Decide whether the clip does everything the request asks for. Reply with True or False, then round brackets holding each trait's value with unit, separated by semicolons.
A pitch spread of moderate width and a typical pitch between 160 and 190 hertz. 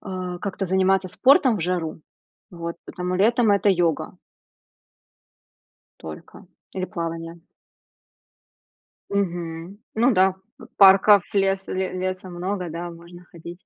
False (2.2 semitones; 185 Hz)